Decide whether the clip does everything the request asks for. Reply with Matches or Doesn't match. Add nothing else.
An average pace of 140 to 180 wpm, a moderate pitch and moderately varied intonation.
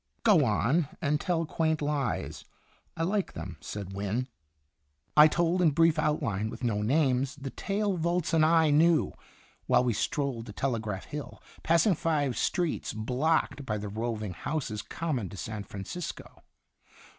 Doesn't match